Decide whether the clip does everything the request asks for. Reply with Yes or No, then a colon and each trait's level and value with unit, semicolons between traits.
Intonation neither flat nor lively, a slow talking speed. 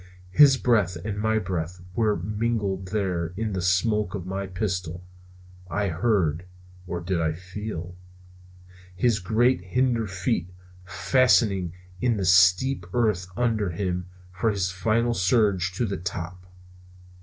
Yes: average, 3.5 semitones; slow, 130 wpm